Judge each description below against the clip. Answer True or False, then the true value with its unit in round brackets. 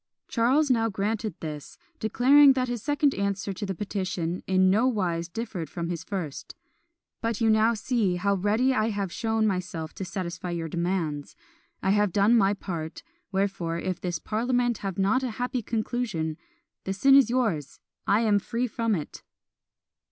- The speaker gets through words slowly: False (165 wpm)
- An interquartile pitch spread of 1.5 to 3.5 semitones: False (4.5 semitones)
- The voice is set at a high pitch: True (200 Hz)